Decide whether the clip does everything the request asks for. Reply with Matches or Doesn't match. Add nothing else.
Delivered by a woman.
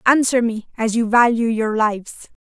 Matches